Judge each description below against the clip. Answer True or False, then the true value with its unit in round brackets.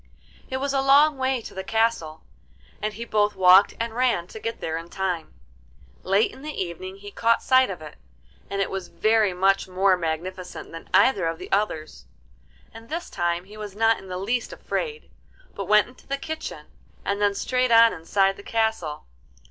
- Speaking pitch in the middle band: False (205 Hz)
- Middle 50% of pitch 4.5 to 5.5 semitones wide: False (4.0 semitones)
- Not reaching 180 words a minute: False (190 wpm)